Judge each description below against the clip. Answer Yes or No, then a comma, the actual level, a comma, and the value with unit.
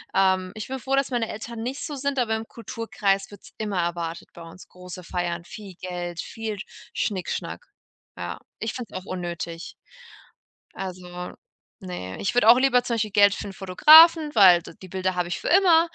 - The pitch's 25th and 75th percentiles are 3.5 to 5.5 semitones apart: Yes, average, 5.1 semitones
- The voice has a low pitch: No, high, 195 Hz